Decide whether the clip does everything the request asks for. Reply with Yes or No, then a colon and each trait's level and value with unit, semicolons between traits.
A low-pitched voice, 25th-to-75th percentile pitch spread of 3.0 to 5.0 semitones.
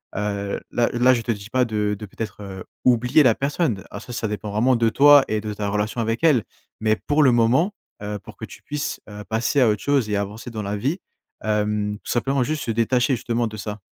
Yes: low, 115 Hz; average, 3.5 semitones